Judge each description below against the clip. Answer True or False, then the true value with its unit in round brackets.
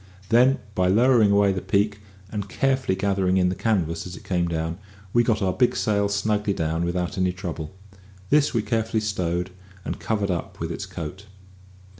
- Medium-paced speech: True (180 wpm)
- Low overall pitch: True (100 Hz)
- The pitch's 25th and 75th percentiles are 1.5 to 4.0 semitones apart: True (3.3 semitones)